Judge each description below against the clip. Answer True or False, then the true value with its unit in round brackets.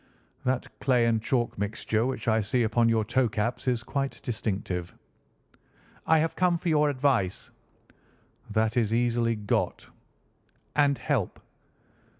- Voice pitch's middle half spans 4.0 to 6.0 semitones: False (3.3 semitones)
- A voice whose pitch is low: True (120 Hz)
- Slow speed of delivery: True (130 wpm)